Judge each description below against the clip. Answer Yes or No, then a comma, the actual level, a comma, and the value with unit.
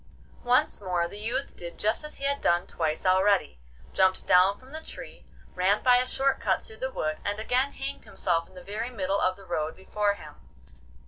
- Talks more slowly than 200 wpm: No, fast, 205 wpm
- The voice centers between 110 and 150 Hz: No, high, 200 Hz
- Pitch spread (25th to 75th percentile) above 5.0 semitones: Yes, wide, 5.4 semitones